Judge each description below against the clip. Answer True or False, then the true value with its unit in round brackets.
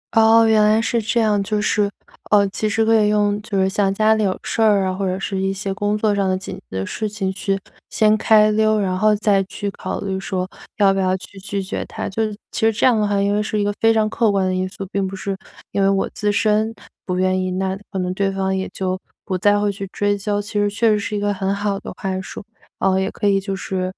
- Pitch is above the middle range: True (200 Hz)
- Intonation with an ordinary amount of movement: False (1.7 semitones)